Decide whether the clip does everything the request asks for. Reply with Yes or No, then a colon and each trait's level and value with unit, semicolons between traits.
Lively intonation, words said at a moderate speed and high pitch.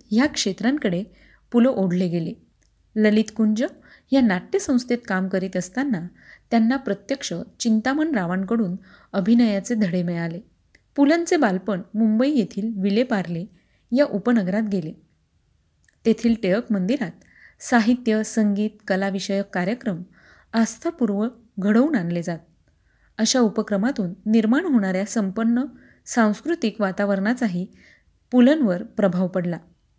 No: average, 4.0 semitones; average, 100 wpm; high, 215 Hz